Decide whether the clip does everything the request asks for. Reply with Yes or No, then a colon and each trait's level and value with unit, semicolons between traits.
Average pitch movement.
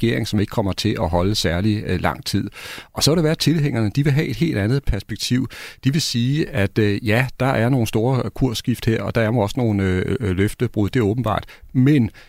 Yes: average, 4.3 semitones